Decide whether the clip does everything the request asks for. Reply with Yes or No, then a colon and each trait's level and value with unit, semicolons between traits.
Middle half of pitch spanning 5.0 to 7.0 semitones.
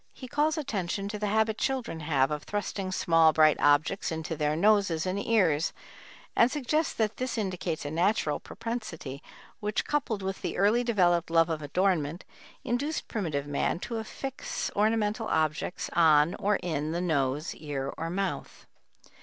Yes: wide, 5.6 semitones